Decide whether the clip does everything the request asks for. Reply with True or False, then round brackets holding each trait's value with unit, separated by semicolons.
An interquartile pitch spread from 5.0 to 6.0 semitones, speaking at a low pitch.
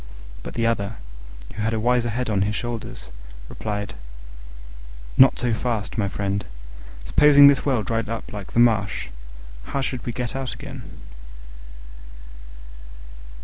False (3.1 semitones; 115 Hz)